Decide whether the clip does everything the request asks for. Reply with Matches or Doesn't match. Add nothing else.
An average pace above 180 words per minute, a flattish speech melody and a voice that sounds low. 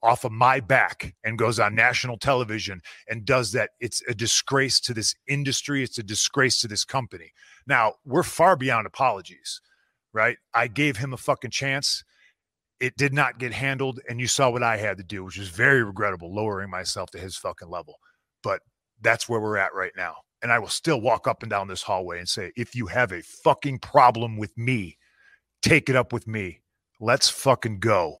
Doesn't match